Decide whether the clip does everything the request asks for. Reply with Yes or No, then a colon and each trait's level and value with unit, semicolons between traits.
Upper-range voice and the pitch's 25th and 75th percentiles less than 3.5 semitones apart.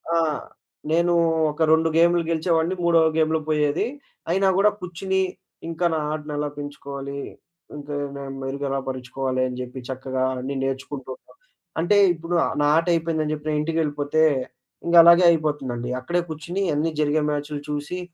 No: medium, 150 Hz; average, 3.1 semitones